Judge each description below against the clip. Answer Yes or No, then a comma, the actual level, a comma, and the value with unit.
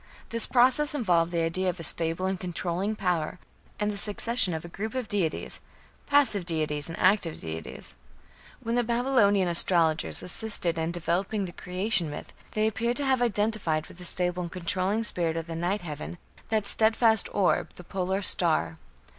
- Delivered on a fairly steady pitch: No, average, 4.4 semitones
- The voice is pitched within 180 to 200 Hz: Yes, medium, 185 Hz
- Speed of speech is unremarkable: Yes, average, 170 wpm